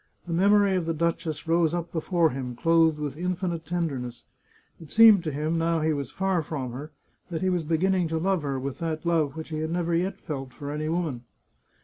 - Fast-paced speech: Yes, fast, 215 wpm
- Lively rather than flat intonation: No, narrow, 2.6 semitones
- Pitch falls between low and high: Yes, medium, 165 Hz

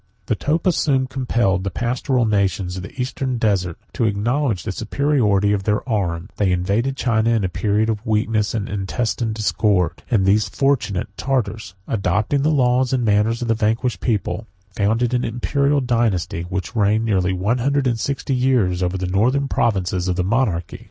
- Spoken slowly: No, average, 175 wpm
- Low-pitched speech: Yes, low, 110 Hz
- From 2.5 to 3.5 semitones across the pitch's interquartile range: No, average, 4.3 semitones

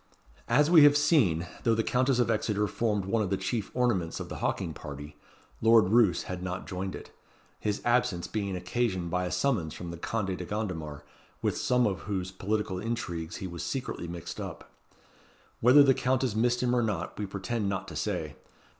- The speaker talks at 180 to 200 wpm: Yes, average, 190 wpm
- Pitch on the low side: Yes, low, 105 Hz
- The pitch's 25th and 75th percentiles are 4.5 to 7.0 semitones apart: Yes, average, 4.8 semitones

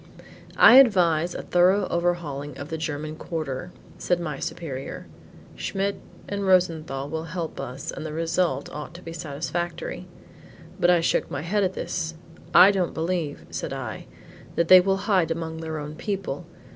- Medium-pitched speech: Yes, medium, 165 Hz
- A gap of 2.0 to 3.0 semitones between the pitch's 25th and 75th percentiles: Yes, average, 2.7 semitones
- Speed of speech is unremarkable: Yes, average, 160 wpm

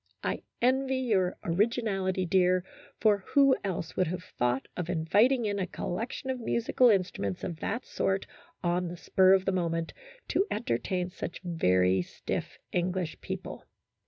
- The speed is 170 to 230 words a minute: No, average, 150 wpm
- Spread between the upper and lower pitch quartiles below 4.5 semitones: Yes, average, 4.0 semitones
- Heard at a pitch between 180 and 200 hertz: Yes, medium, 185 Hz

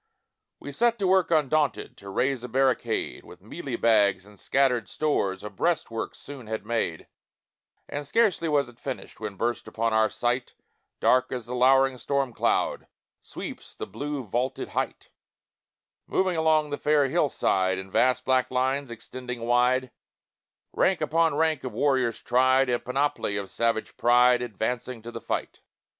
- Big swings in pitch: No, average, 3.5 semitones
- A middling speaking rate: Yes, average, 155 wpm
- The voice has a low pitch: Yes, low, 125 Hz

